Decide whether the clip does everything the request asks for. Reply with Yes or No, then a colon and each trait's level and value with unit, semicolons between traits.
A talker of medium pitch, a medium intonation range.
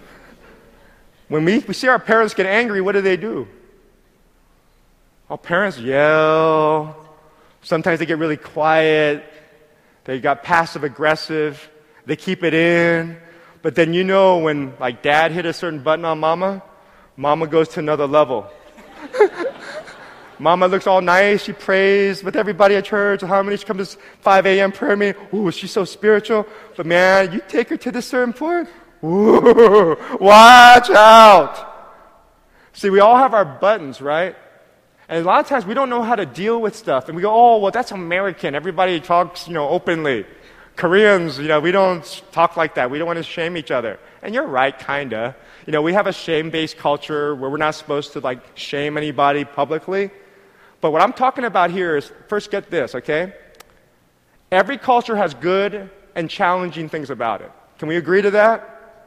Yes: medium, 175 Hz; average, 4.7 semitones